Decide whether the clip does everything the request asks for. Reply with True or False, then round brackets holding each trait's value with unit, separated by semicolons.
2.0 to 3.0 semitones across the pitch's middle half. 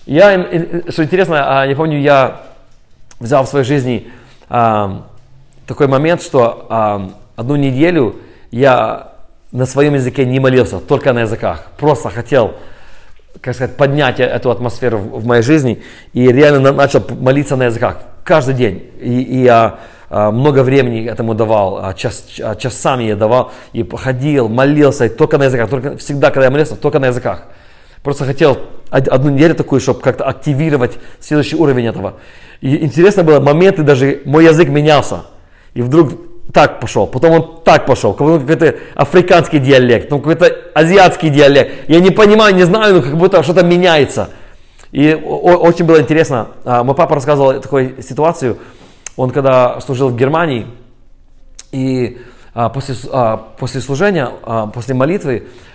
False (4.1 semitones)